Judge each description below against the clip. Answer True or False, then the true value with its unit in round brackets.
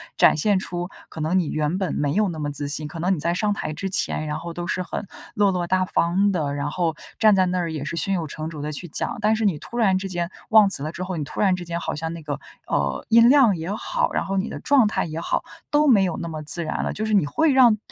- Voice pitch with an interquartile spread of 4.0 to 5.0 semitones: True (4.4 semitones)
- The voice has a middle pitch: True (175 Hz)